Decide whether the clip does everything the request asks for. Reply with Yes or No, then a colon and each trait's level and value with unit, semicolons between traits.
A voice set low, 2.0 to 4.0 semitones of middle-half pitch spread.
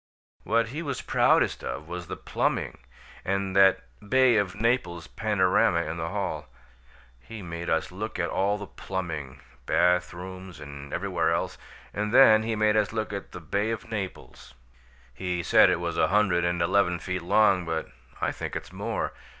Yes: very low, 95 Hz; average, 3.5 semitones